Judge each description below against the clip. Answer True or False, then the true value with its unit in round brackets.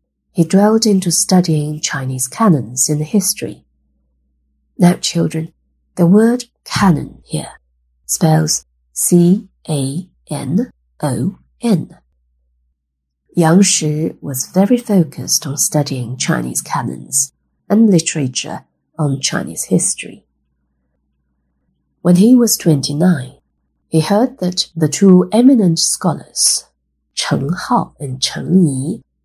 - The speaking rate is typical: False (95 wpm)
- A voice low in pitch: False (150 Hz)